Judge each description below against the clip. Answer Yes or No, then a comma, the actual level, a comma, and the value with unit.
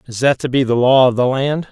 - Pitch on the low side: Yes, low, 130 Hz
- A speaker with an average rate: No, fast, 315 wpm